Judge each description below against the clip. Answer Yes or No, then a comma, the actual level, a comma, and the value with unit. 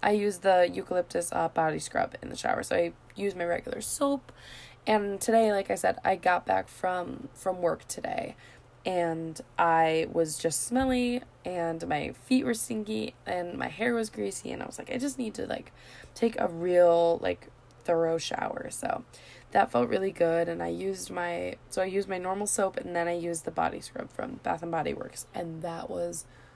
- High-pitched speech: No, medium, 175 Hz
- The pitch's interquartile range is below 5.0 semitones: Yes, average, 3.9 semitones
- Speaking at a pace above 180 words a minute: Yes, average, 200 wpm